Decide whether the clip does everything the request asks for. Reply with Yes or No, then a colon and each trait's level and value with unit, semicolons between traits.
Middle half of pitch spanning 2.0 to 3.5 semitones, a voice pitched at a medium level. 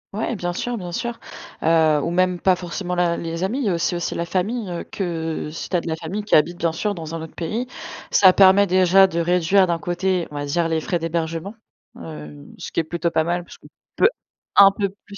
Yes: average, 2.7 semitones; medium, 175 Hz